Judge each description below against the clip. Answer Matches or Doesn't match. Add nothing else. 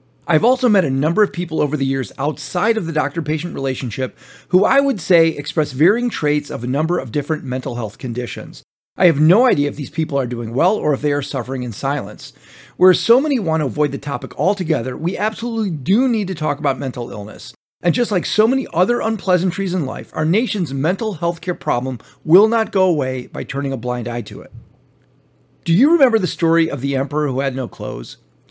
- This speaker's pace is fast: Matches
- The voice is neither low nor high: Matches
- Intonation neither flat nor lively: Doesn't match